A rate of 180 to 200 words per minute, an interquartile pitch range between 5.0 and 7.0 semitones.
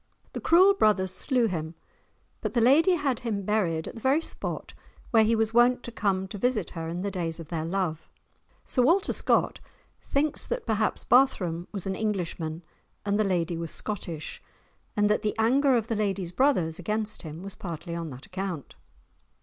Yes: average, 185 wpm; wide, 5.6 semitones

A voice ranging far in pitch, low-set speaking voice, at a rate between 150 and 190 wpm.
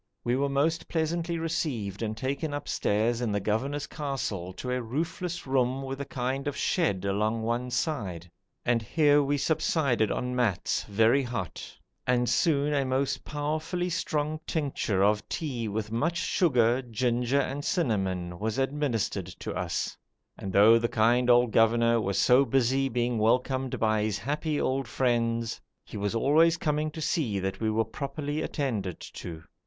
No: average, 4.7 semitones; low, 125 Hz; average, 160 wpm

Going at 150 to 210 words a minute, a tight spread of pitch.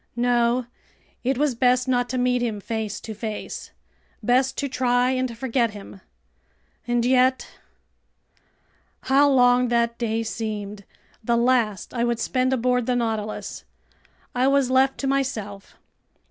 No: slow, 135 wpm; narrow, 2.2 semitones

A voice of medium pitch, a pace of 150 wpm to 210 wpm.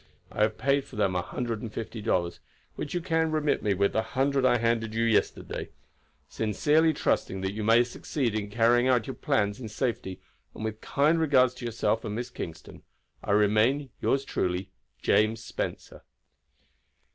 No: low, 115 Hz; average, 175 wpm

